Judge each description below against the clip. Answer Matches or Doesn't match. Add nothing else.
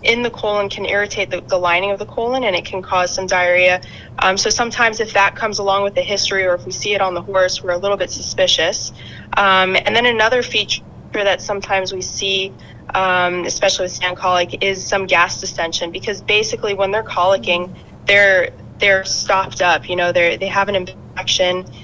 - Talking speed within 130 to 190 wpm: Doesn't match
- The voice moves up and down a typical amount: Doesn't match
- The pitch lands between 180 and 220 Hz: Matches